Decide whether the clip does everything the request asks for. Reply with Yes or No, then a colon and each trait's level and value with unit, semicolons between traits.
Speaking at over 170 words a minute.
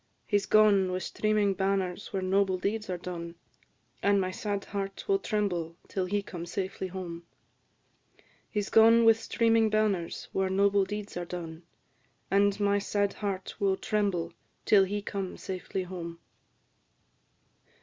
No: average, 150 wpm